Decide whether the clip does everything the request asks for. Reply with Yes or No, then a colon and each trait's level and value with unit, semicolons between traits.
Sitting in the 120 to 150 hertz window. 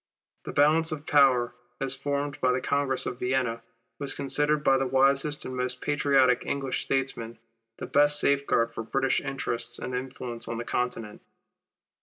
Yes: low, 135 Hz